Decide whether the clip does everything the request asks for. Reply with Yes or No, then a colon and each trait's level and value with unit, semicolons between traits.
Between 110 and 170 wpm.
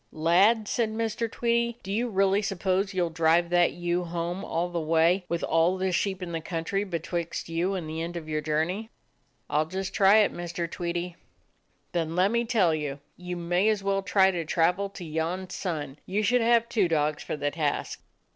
No: fast, 205 wpm